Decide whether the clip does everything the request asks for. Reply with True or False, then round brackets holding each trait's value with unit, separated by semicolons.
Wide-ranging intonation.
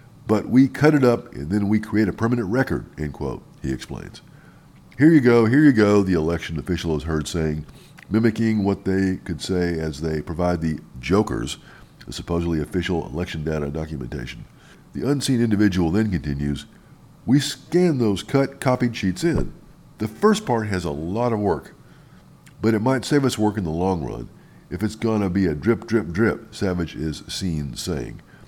True (6.2 semitones)